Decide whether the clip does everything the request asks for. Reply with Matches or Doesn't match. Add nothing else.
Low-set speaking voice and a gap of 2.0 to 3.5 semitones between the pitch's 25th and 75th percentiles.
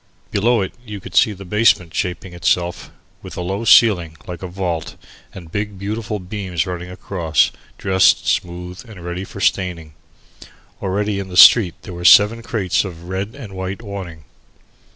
Matches